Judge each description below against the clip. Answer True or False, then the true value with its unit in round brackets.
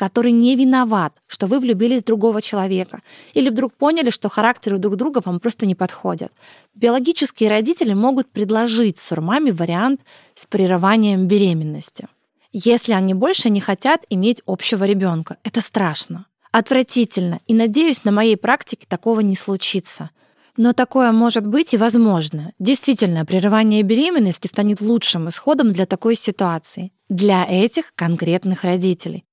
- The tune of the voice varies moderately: True (4.1 semitones)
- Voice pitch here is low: False (215 Hz)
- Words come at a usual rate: True (135 wpm)